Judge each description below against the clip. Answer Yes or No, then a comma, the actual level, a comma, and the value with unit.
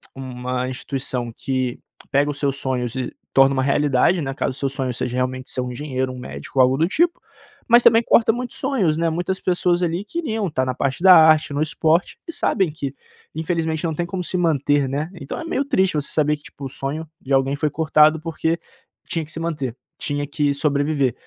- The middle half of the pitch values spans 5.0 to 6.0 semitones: No, average, 4.0 semitones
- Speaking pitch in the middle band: Yes, medium, 150 Hz